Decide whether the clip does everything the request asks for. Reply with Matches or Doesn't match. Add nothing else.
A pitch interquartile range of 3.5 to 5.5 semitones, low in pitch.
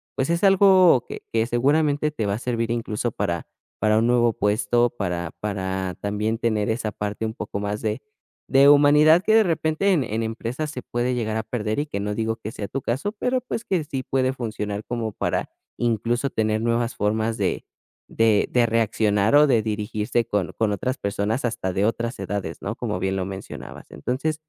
Matches